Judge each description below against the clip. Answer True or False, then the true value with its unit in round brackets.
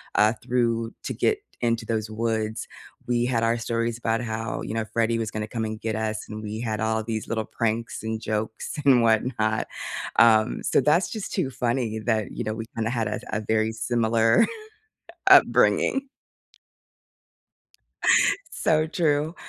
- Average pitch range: False (1.4 semitones)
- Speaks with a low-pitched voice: True (115 Hz)